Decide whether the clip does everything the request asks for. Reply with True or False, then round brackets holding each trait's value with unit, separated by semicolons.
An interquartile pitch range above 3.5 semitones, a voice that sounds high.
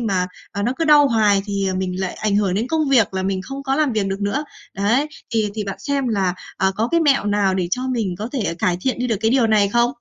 True (4.6 semitones; 215 Hz)